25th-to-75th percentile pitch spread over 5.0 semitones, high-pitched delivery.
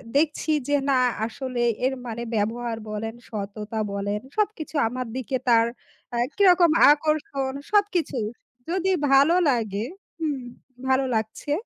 Yes: wide, 5.5 semitones; very high, 260 Hz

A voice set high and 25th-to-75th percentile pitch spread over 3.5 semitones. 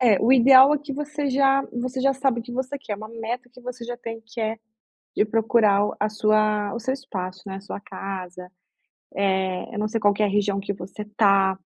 Yes: high, 220 Hz; average, 3.9 semitones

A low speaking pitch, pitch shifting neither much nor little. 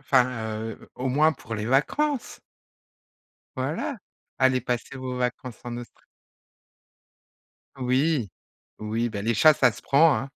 Yes: low, 125 Hz; average, 3.1 semitones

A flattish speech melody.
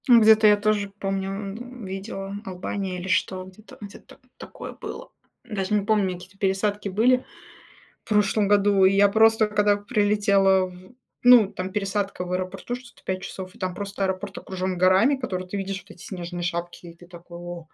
Yes: narrow, 2.0 semitones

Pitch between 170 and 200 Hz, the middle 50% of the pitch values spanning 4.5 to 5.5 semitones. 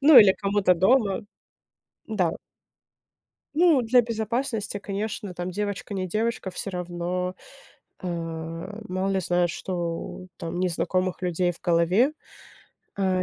No: high, 190 Hz; average, 3.2 semitones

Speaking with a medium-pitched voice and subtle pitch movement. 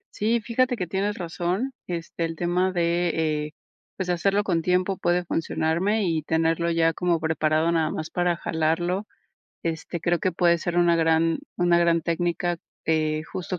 Yes: medium, 170 Hz; narrow, 1.8 semitones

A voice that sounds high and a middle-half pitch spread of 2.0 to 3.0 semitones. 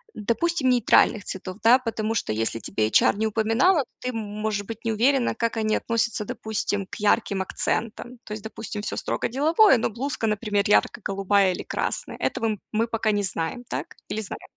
Yes: high, 220 Hz; narrow, 2.4 semitones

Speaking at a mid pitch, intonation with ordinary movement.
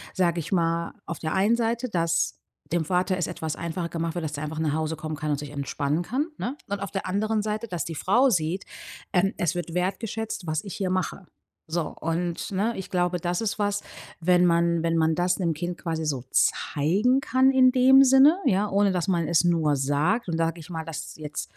Yes: medium, 175 Hz; average, 3.9 semitones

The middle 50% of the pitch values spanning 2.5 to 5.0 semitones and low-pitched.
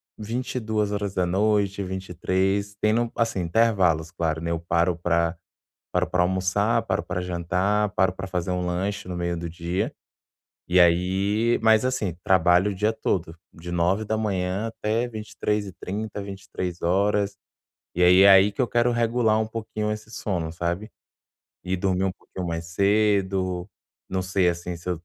Yes: average, 3.1 semitones; very low, 95 Hz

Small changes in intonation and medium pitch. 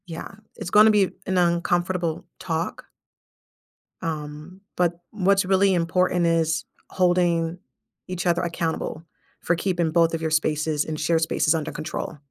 Yes: narrow, 2.1 semitones; medium, 170 Hz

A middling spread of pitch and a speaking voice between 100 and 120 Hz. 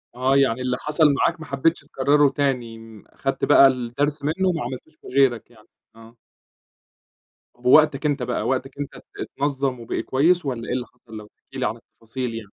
No: average, 3.1 semitones; low, 135 Hz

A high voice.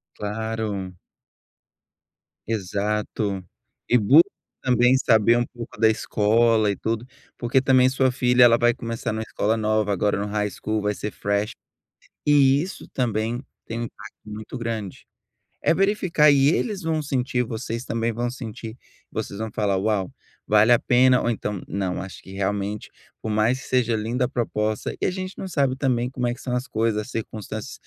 No: low, 115 Hz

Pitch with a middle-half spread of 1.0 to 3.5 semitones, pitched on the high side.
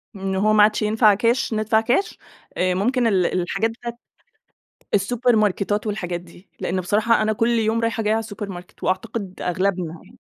Yes: average, 3.1 semitones; high, 210 Hz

